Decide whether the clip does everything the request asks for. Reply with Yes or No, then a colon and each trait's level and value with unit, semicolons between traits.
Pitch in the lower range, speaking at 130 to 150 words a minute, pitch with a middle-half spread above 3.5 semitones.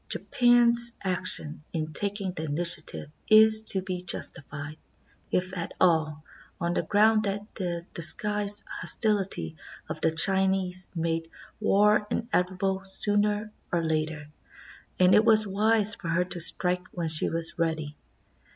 No: medium, 185 Hz; average, 140 wpm; average, 4.1 semitones